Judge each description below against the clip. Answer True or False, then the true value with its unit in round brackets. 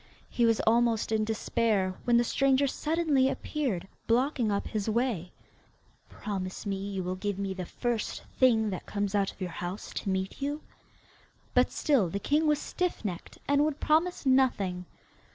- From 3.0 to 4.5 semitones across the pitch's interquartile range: False (5.6 semitones)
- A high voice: True (225 Hz)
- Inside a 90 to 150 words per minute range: False (165 wpm)